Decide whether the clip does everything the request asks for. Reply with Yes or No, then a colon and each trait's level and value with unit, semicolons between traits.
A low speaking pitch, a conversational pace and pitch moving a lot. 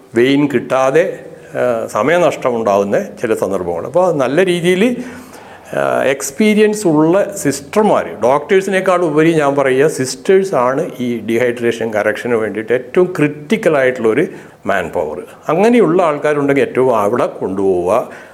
No: medium, 155 Hz; average, 95 wpm; wide, 6.8 semitones